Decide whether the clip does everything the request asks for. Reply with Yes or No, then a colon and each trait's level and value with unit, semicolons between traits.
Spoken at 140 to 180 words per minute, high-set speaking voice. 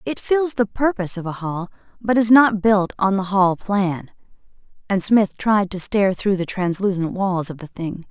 No: average, 200 wpm; high, 195 Hz